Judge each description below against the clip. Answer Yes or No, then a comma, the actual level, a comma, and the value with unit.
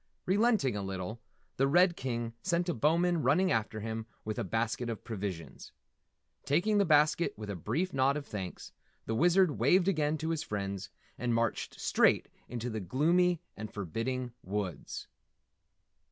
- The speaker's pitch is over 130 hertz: No, low, 125 Hz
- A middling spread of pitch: No, wide, 7.6 semitones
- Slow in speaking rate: No, average, 155 wpm